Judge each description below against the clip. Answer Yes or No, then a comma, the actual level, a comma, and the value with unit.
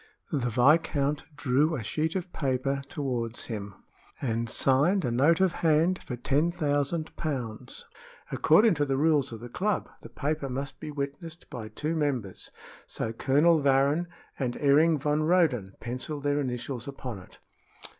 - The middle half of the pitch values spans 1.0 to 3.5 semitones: No, average, 4.0 semitones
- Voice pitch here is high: No, medium, 140 Hz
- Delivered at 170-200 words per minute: No, average, 155 wpm